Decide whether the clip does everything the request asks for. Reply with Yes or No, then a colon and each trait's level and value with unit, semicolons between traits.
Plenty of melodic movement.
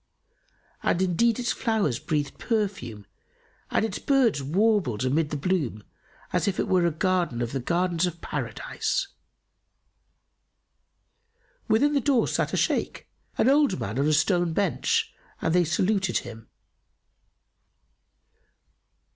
Yes: wide, 6.7 semitones